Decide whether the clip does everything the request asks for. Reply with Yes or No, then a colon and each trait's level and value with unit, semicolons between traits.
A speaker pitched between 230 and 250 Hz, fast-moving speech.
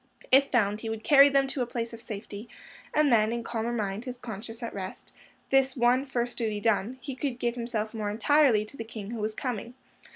Yes: high, 235 Hz; fast, 220 wpm